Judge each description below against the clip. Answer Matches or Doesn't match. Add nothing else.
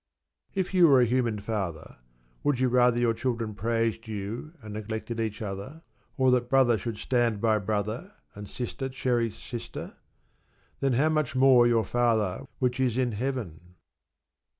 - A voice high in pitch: Doesn't match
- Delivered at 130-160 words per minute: Matches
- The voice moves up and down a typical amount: Matches